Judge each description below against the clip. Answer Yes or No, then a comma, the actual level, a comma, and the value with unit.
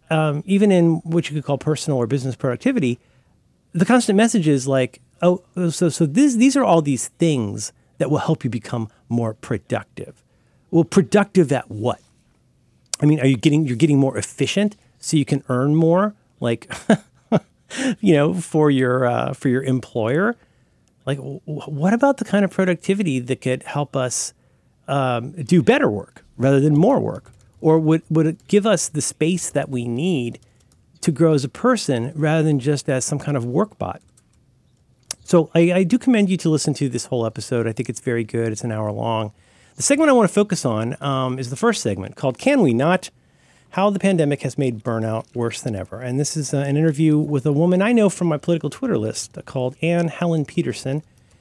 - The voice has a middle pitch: Yes, medium, 145 Hz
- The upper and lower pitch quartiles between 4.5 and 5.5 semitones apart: Yes, average, 5.2 semitones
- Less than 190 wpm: No, average, 200 wpm